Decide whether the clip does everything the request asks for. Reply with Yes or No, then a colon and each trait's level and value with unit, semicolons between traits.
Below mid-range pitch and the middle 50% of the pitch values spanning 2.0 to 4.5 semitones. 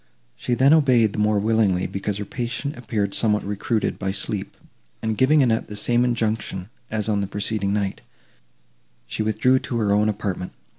Yes: low, 110 Hz; average, 2.7 semitones